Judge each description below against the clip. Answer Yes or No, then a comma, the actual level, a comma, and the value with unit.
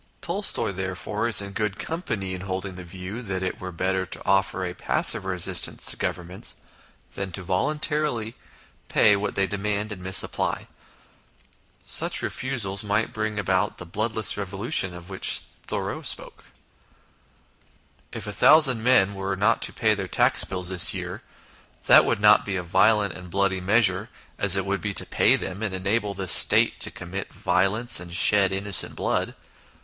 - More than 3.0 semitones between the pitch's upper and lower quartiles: No, narrow, 2.4 semitones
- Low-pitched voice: Yes, low, 100 Hz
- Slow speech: No, average, 170 wpm